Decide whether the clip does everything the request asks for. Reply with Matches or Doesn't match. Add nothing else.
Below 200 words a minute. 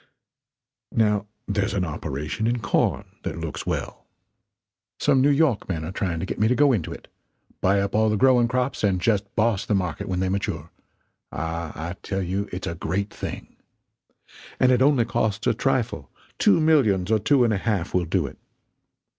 Matches